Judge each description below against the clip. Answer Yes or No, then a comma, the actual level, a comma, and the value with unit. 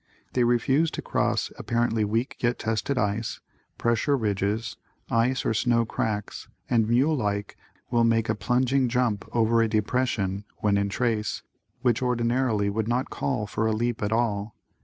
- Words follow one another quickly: No, average, 160 wpm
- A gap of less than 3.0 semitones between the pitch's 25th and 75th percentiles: Yes, narrow, 2.5 semitones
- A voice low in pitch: Yes, low, 115 Hz